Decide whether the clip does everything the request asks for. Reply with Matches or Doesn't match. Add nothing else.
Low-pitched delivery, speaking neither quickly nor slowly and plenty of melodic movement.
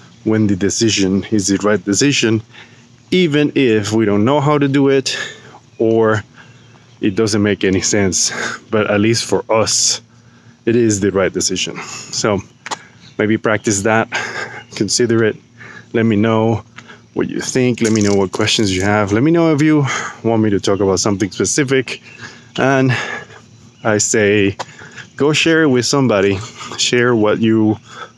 Doesn't match